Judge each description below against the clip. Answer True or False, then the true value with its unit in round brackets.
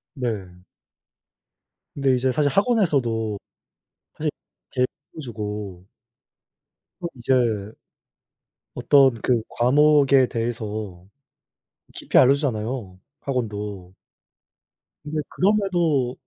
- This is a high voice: False (125 Hz)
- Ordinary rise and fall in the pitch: True (4.8 semitones)